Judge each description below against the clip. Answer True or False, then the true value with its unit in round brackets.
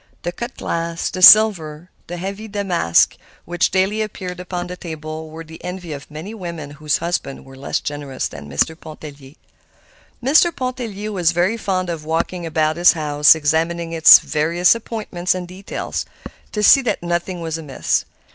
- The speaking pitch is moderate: True (170 Hz)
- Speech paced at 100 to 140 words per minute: False (165 wpm)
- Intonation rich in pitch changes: False (3.2 semitones)